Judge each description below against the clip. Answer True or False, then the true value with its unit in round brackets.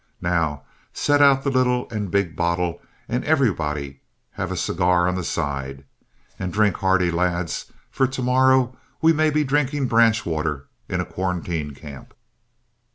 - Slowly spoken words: False (155 wpm)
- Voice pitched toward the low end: True (95 Hz)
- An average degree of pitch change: False (7.7 semitones)